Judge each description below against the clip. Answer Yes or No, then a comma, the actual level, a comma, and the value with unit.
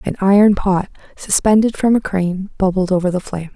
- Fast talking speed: No, average, 185 wpm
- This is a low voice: No, high, 195 Hz